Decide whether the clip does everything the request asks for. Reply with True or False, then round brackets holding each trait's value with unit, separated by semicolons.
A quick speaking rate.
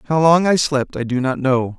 True (270 wpm)